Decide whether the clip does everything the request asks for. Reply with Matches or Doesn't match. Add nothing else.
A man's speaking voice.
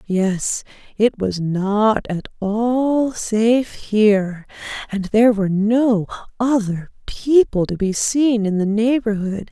Doesn't match